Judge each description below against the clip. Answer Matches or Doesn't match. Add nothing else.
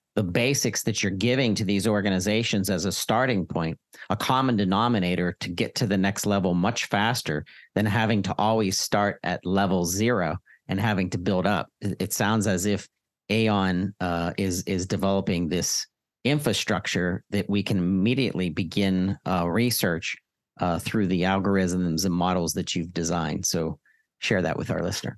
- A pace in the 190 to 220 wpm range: Doesn't match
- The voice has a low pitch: Matches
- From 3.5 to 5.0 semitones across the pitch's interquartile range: Doesn't match